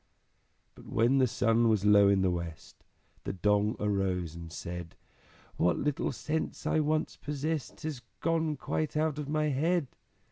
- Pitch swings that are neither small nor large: No, wide, 7.8 semitones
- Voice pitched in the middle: No, low, 120 Hz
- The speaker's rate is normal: Yes, average, 155 wpm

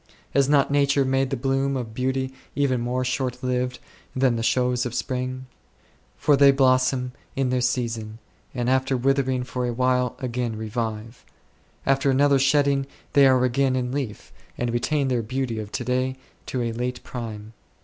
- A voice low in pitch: Yes, low, 130 Hz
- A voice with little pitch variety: Yes, narrow, 1.7 semitones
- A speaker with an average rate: Yes, average, 165 wpm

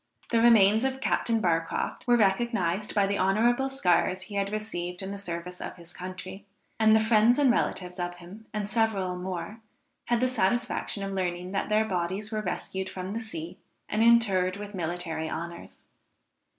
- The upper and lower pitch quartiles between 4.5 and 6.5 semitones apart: No, average, 3.6 semitones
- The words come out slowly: No, average, 175 wpm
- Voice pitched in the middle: No, high, 195 Hz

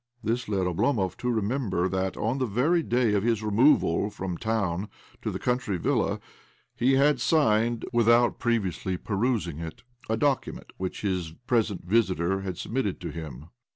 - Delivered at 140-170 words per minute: Yes, average, 155 wpm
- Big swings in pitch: No, average, 4.5 semitones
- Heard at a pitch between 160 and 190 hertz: No, low, 105 Hz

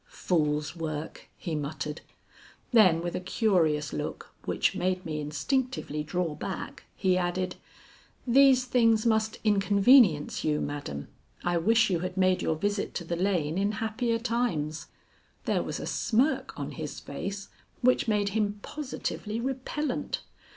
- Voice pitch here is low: No, high, 190 Hz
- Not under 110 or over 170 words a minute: Yes, average, 140 wpm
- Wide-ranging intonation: Yes, wide, 6.0 semitones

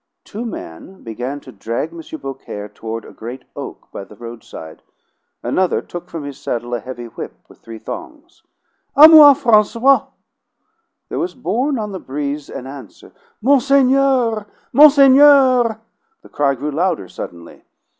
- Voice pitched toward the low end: No, medium, 175 Hz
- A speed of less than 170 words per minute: Yes, average, 145 wpm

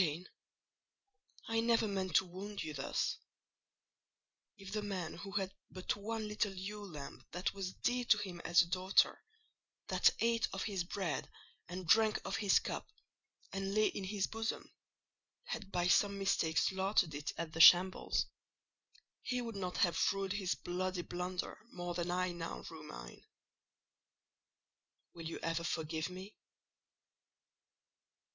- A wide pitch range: No, average, 2.8 semitones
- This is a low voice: No, high, 190 Hz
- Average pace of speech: Yes, average, 145 wpm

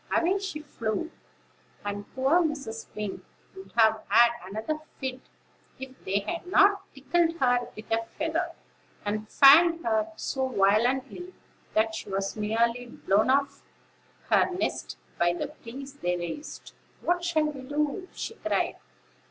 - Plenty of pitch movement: Yes, wide, 7.0 semitones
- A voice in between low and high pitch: No, very high, 265 Hz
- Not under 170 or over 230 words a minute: No, slow, 135 wpm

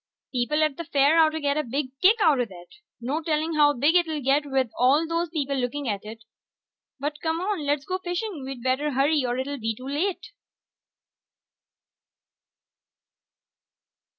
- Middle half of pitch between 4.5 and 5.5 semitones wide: No, average, 3.5 semitones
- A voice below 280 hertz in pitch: No, very high, 290 Hz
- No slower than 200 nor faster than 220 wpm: No, average, 160 wpm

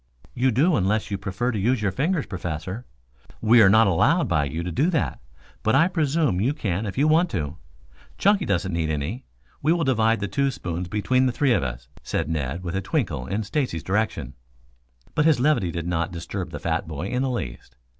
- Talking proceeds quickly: Yes, fast, 210 wpm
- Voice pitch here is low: Yes, low, 105 Hz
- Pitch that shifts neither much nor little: No, wide, 7.7 semitones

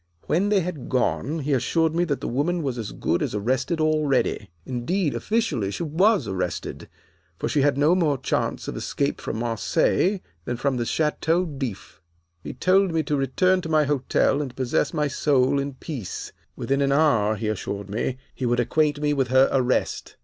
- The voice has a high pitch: No, medium, 140 Hz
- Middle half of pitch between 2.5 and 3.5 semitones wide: No, average, 4.3 semitones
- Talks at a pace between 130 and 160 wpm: No, average, 185 wpm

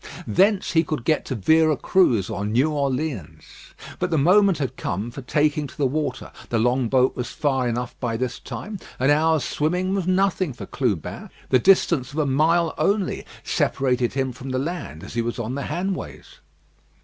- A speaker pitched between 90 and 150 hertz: Yes, medium, 140 Hz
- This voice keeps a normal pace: Yes, average, 185 wpm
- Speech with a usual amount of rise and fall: Yes, average, 4.7 semitones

